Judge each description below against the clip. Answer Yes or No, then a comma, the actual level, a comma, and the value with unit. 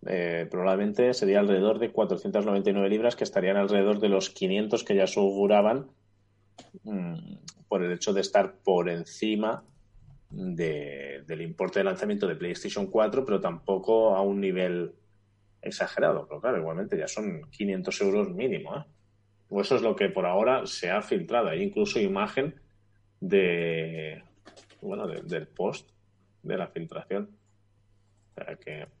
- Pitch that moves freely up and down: Yes, wide, 6.0 semitones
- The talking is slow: No, average, 150 wpm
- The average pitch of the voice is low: Yes, low, 100 Hz